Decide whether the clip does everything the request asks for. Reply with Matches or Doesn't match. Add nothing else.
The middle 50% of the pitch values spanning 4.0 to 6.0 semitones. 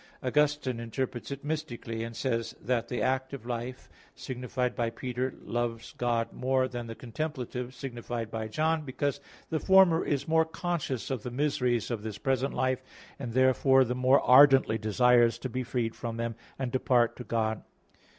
Doesn't match